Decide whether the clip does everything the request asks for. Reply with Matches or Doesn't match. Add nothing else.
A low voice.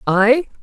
Doesn't match